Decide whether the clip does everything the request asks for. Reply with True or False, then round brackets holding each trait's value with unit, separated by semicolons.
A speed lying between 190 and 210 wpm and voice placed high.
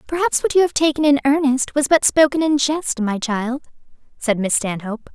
True (200 wpm; 275 Hz)